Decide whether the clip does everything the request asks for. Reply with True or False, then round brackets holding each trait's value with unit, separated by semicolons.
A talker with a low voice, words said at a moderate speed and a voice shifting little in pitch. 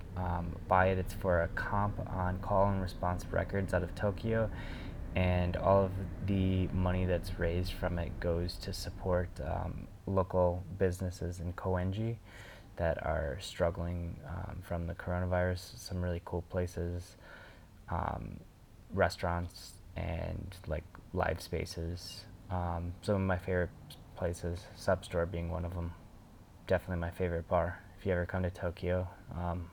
True (90 Hz; 145 wpm; 1.7 semitones)